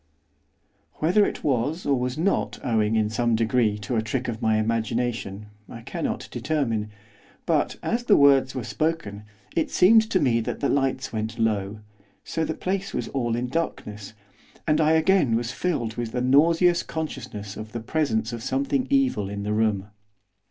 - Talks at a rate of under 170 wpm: No, average, 175 wpm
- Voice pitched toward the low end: Yes, low, 125 Hz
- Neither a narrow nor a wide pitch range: No, wide, 6.3 semitones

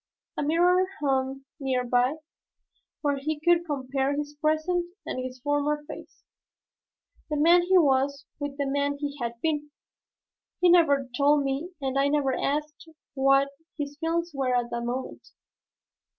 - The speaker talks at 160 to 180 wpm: No, average, 150 wpm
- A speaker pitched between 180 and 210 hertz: No, very high, 285 Hz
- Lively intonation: No, narrow, 2.4 semitones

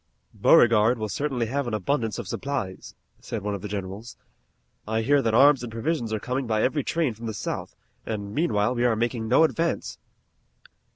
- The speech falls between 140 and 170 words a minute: No, average, 185 wpm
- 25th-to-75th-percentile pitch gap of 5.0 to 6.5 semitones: No, average, 4.0 semitones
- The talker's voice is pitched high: No, low, 115 Hz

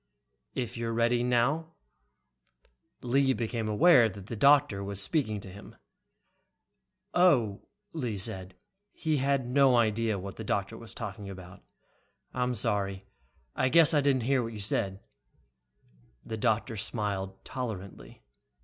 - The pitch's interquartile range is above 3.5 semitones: Yes, average, 4.5 semitones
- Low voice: Yes, low, 115 Hz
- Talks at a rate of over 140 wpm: No, slow, 135 wpm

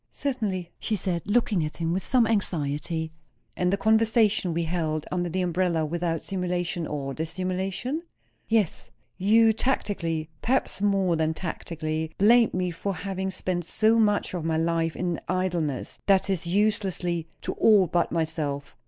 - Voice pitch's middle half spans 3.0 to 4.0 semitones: Yes, average, 3.6 semitones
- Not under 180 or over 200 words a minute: No, average, 150 wpm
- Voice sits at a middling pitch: Yes, medium, 180 Hz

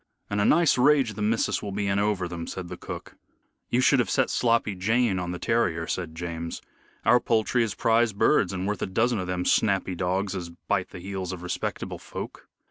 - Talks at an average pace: No, fast, 210 wpm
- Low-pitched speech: Yes, low, 100 Hz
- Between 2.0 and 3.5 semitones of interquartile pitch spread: No, average, 4.1 semitones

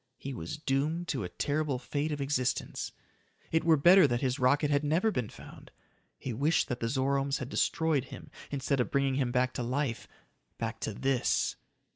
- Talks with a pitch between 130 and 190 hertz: Yes, medium, 140 Hz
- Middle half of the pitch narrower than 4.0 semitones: Yes, average, 2.9 semitones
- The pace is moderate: Yes, average, 185 wpm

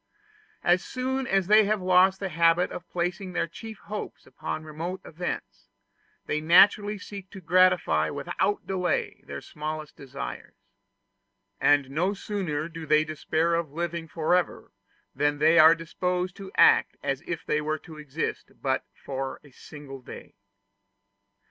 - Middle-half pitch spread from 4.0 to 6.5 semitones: No, average, 3.5 semitones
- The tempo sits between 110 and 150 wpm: Yes, average, 145 wpm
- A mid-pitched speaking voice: Yes, medium, 170 Hz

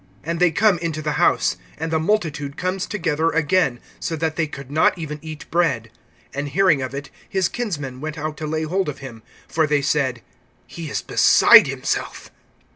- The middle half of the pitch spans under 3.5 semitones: Yes, average, 2.8 semitones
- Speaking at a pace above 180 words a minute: Yes, average, 190 wpm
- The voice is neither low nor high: Yes, medium, 155 Hz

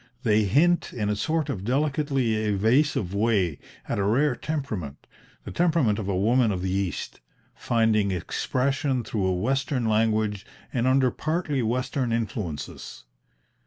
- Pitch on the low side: Yes, low, 115 Hz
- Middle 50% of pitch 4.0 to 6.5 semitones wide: Yes, average, 4.9 semitones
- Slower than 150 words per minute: Yes, average, 140 wpm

